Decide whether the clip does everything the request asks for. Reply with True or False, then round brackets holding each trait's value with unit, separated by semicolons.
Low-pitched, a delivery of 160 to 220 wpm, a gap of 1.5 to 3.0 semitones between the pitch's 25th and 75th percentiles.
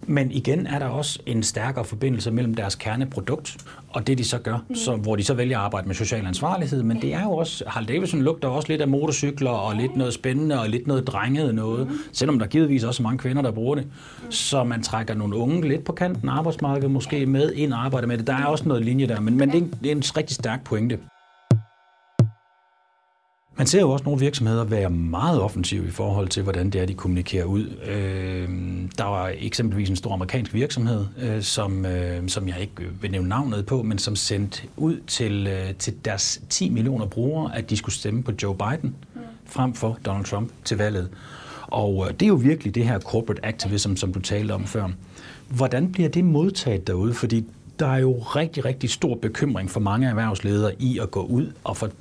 False (120 Hz; 210 wpm; 5.1 semitones)